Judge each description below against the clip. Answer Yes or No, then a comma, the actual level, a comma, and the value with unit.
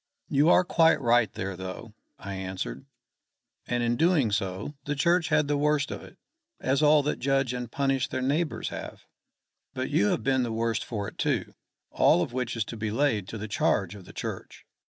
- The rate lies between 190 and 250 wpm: Yes, average, 200 wpm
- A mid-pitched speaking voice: No, low, 120 Hz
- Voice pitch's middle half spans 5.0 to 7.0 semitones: Yes, wide, 5.4 semitones